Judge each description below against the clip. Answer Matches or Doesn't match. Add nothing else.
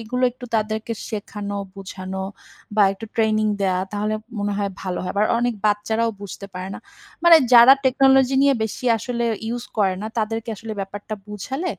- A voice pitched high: Matches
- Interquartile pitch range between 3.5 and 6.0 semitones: Doesn't match